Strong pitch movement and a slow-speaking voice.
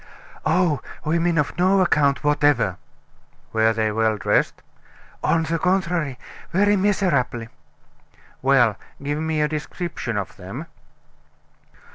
Yes: wide, 6.3 semitones; slow, 110 wpm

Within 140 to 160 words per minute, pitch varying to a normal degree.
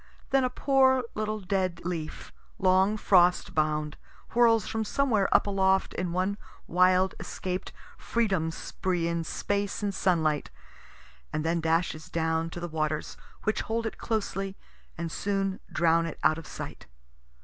Yes: average, 145 wpm; average, 3.8 semitones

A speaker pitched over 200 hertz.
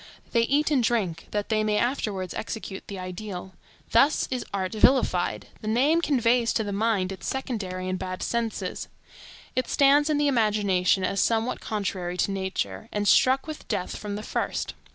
Yes: high, 215 Hz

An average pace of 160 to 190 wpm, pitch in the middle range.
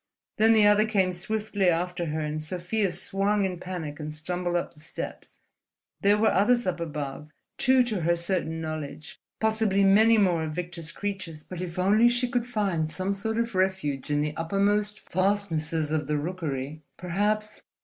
Yes: average, 170 wpm; medium, 180 Hz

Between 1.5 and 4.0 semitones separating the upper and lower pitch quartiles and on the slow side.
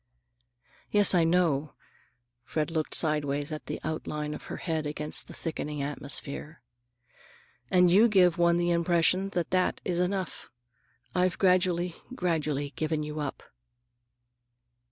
Yes: average, 3.0 semitones; slow, 130 wpm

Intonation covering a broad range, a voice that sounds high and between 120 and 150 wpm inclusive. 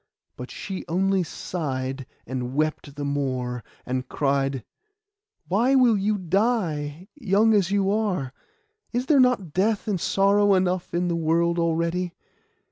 No: wide, 5.9 semitones; medium, 175 Hz; slow, 135 wpm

